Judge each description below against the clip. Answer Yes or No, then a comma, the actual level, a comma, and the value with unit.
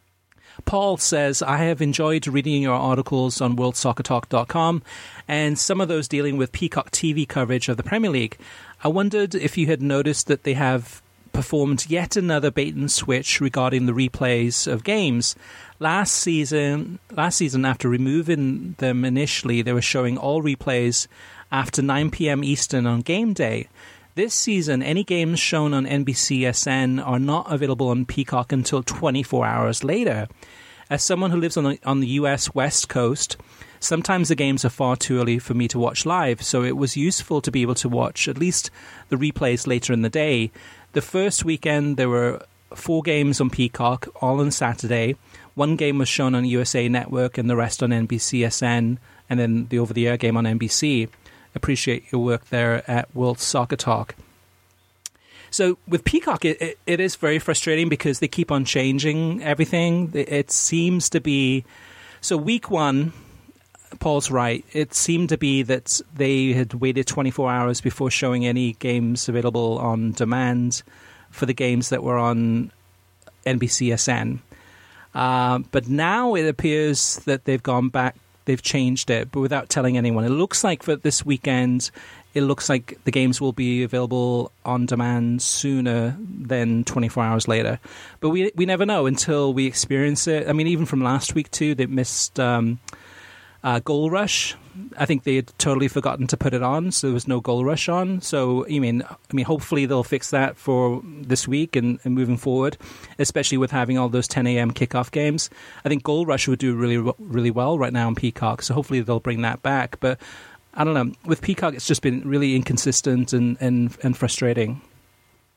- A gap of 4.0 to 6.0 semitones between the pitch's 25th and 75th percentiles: No, average, 3.5 semitones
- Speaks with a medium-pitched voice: No, low, 130 Hz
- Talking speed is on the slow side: No, average, 180 wpm